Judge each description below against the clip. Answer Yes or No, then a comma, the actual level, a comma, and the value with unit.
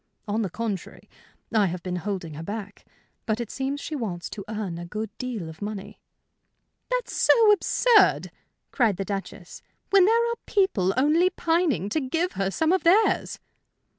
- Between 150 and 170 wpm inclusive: Yes, average, 165 wpm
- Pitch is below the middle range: No, high, 225 Hz